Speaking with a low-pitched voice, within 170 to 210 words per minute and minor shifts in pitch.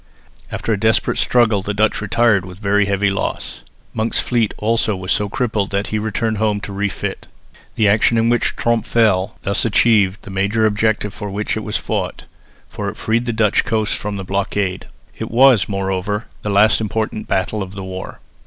Yes: low, 105 Hz; average, 185 wpm; narrow, 2.0 semitones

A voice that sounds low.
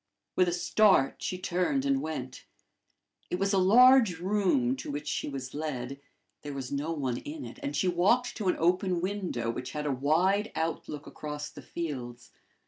No: medium, 170 Hz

